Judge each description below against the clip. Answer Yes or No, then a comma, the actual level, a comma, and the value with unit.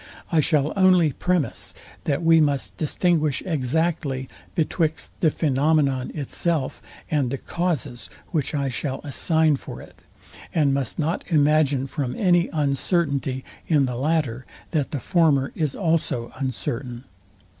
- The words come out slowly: Yes, slow, 130 wpm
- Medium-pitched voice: Yes, medium, 150 Hz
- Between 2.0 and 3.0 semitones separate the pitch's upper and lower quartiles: No, average, 3.4 semitones